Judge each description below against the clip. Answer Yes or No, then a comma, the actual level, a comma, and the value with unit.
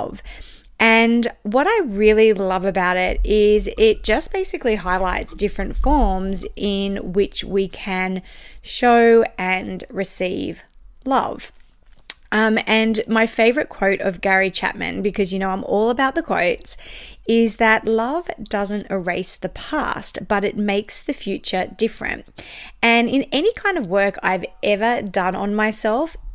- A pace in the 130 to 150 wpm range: Yes, average, 140 wpm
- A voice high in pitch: Yes, high, 210 Hz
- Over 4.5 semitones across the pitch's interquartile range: No, average, 3.1 semitones